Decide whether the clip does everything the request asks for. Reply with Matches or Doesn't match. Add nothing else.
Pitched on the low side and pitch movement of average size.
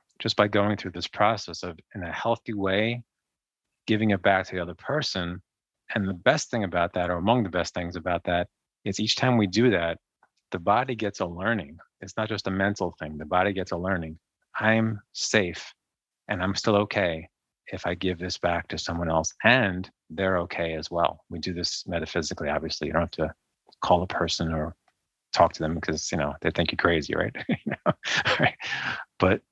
Matches